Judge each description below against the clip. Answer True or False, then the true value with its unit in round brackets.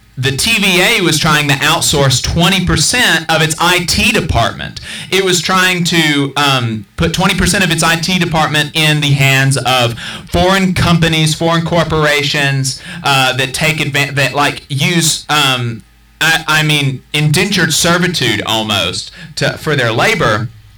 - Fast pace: False (140 wpm)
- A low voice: False (150 Hz)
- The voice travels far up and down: False (4.0 semitones)